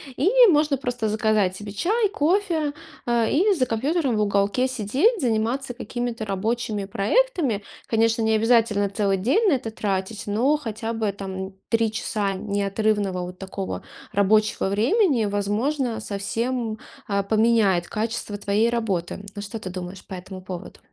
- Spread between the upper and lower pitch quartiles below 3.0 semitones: No, average, 3.7 semitones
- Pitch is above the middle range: Yes, high, 220 Hz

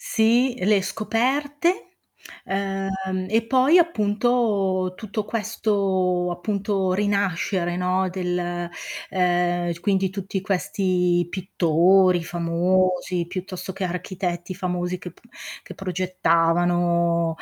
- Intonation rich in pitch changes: No, narrow, 2.4 semitones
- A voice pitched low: No, medium, 185 Hz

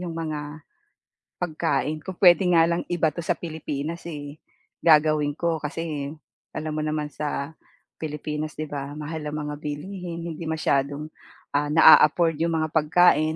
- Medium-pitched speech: Yes, medium, 155 Hz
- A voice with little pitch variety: Yes, narrow, 1.8 semitones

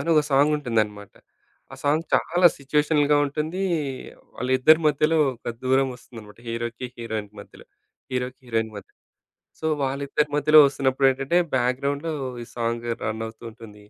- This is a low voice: Yes, low, 130 Hz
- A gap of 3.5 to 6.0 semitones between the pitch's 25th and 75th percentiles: Yes, average, 4.1 semitones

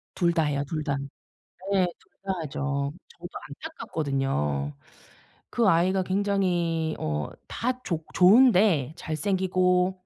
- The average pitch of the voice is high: No, medium, 170 Hz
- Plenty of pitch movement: No, average, 4.8 semitones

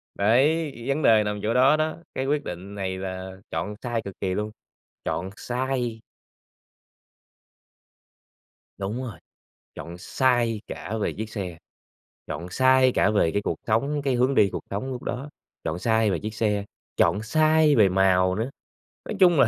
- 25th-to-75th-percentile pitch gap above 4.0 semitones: Yes, average, 5.1 semitones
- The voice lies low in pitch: Yes, low, 110 Hz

